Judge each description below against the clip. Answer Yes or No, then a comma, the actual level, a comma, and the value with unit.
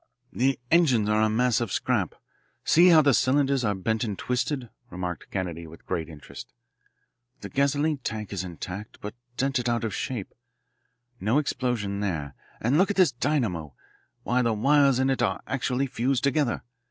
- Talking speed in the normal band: Yes, average, 165 wpm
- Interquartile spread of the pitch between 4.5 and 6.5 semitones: Yes, average, 5.2 semitones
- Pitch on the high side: No, low, 120 Hz